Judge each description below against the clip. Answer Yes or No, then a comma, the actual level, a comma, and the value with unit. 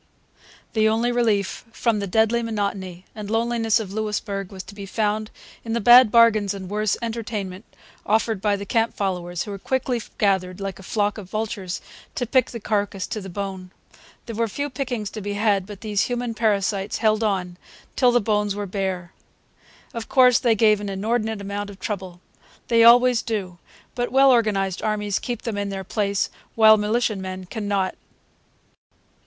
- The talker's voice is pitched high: Yes, high, 210 Hz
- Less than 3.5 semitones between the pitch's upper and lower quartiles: Yes, narrow, 2.6 semitones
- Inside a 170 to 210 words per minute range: Yes, average, 175 wpm